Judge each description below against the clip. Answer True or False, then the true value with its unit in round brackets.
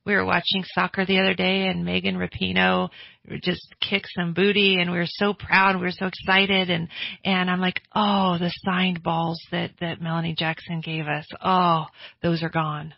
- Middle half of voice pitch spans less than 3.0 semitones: True (2.6 semitones)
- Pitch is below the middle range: False (175 Hz)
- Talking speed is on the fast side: False (190 wpm)